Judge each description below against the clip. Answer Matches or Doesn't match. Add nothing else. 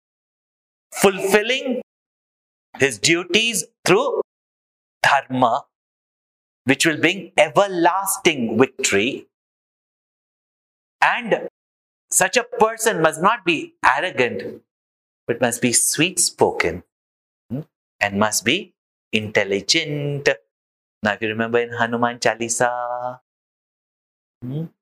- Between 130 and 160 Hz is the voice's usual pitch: Matches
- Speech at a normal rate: Doesn't match